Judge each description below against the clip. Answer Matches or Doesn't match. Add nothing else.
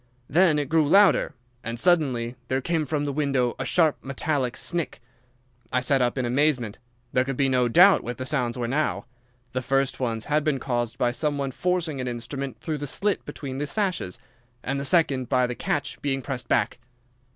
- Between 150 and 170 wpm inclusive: Doesn't match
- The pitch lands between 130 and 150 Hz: Matches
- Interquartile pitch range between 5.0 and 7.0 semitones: Doesn't match